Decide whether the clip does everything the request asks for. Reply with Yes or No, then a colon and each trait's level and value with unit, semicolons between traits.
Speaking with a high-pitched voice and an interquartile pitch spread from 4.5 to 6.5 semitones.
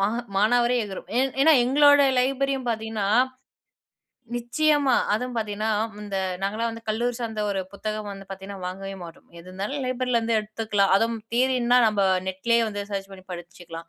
No: high, 220 Hz; average, 3.8 semitones